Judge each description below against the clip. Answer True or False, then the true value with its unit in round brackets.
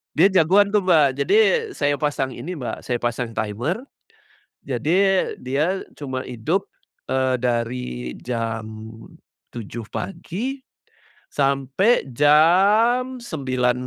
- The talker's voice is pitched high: False (140 Hz)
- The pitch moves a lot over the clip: True (7.1 semitones)